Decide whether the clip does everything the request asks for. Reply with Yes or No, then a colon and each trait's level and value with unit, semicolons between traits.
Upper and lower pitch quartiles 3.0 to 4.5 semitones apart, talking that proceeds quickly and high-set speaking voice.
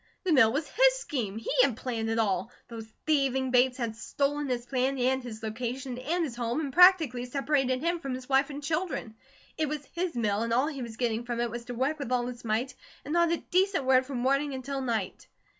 Yes: average, 3.5 semitones; fast, 225 wpm; very high, 260 Hz